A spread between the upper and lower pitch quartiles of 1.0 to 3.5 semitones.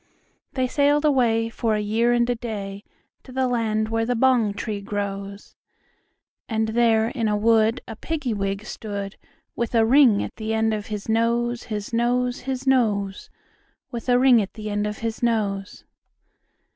Yes: narrow, 2.4 semitones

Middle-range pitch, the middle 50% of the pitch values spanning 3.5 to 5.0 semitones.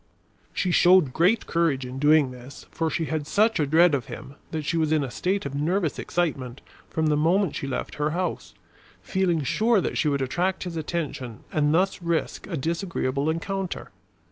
Yes: medium, 160 Hz; average, 3.9 semitones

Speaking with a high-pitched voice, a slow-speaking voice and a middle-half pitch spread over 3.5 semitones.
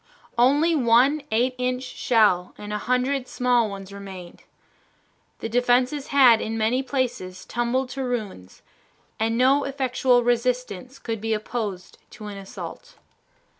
No: high, 245 Hz; slow, 130 wpm; average, 3.1 semitones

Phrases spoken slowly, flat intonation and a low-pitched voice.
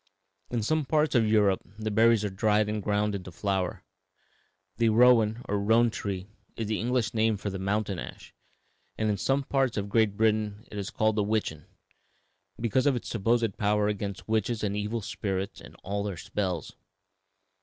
No: average, 175 wpm; narrow, 2.1 semitones; low, 105 Hz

